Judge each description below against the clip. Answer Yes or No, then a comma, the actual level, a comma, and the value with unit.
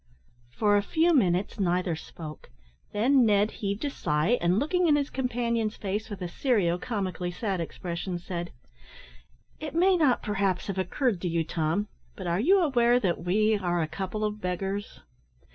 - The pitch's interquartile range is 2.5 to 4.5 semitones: No, average, 5.2 semitones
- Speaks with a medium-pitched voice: No, high, 200 Hz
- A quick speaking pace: No, average, 170 wpm